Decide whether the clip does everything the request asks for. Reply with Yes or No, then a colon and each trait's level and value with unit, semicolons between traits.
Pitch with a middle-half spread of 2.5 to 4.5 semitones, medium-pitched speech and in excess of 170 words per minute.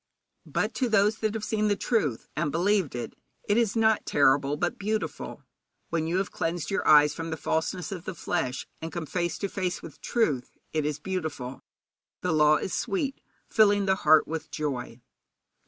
No: average, 5.1 semitones; medium, 170 Hz; average, 185 wpm